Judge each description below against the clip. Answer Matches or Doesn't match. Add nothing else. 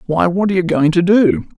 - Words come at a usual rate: Doesn't match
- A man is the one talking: Matches